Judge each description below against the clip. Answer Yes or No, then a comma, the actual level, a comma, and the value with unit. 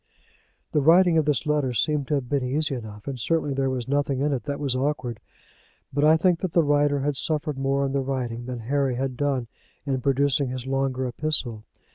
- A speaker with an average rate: No, fast, 210 wpm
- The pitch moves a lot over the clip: No, narrow, 2.4 semitones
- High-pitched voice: No, low, 135 Hz